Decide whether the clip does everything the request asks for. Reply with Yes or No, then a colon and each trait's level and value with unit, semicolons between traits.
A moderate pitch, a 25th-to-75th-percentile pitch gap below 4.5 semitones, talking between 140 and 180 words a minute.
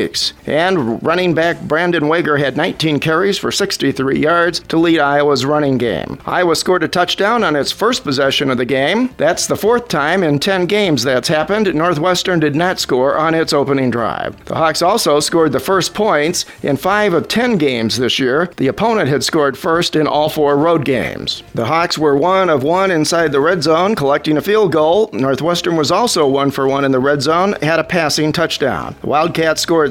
No: medium, 160 Hz; average, 3.7 semitones; average, 200 wpm